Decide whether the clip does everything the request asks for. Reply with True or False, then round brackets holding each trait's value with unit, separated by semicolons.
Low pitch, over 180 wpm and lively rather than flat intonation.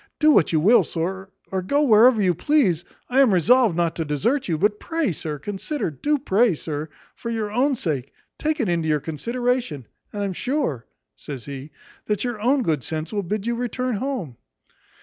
False (205 Hz; 190 wpm; 7.6 semitones)